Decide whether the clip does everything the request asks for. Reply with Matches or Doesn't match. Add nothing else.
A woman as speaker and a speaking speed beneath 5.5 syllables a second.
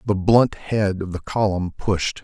Doesn't match